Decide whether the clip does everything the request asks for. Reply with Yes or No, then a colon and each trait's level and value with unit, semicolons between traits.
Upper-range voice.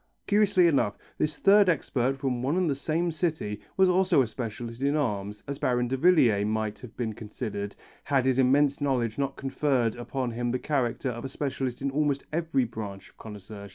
No: low, 130 Hz